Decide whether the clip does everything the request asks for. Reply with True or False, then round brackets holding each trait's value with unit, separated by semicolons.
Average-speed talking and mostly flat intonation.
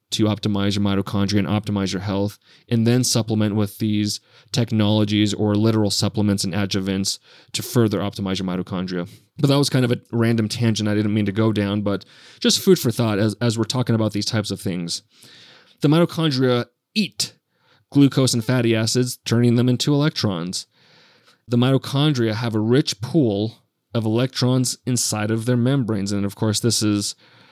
False (175 wpm; 3.2 semitones)